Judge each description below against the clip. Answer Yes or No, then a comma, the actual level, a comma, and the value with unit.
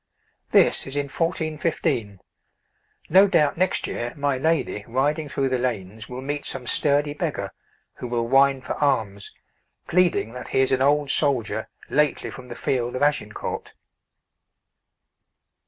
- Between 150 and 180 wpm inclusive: No, average, 140 wpm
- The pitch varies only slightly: No, average, 3.4 semitones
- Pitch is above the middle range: No, low, 135 Hz